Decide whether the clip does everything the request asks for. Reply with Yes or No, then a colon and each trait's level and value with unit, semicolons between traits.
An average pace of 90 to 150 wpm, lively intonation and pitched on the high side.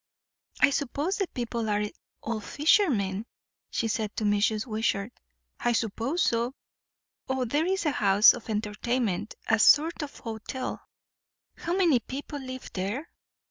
No: average, 140 wpm; average, 5.0 semitones; high, 235 Hz